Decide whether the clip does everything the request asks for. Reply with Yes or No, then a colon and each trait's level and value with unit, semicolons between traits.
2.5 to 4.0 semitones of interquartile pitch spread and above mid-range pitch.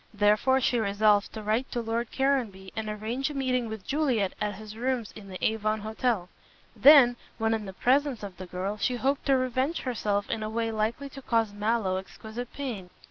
Yes: average, 3.5 semitones; high, 225 Hz